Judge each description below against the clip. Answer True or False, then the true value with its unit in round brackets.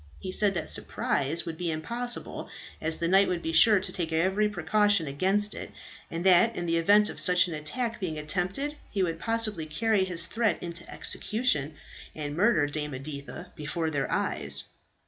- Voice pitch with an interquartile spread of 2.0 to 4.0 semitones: False (4.7 semitones)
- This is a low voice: False (175 Hz)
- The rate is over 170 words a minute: True (180 wpm)